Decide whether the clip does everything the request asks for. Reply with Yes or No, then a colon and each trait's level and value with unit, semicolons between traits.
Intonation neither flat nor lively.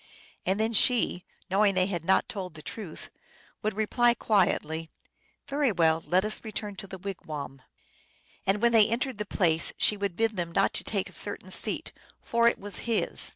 Yes: average, 3.8 semitones